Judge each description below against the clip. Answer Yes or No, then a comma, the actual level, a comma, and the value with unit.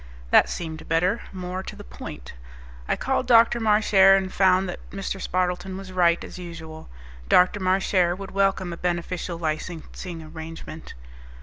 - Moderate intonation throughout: No, narrow, 2.3 semitones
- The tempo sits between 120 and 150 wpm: Yes, average, 145 wpm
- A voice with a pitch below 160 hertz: No, medium, 180 Hz